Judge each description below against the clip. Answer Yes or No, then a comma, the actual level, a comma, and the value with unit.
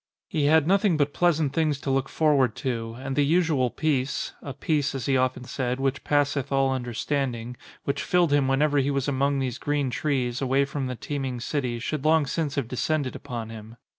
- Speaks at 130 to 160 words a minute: No, fast, 205 wpm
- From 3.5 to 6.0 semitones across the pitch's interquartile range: No, narrow, 2.4 semitones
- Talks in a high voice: No, medium, 140 Hz